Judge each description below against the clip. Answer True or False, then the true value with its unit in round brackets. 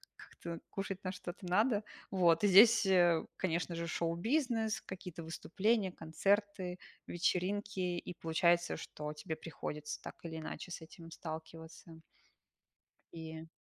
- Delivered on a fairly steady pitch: False (3.3 semitones)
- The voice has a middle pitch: True (175 Hz)